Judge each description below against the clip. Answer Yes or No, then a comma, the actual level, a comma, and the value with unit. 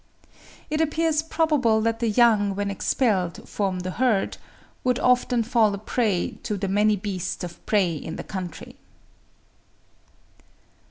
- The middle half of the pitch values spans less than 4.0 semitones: No, average, 4.3 semitones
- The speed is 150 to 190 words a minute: No, average, 140 wpm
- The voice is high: Yes, high, 215 Hz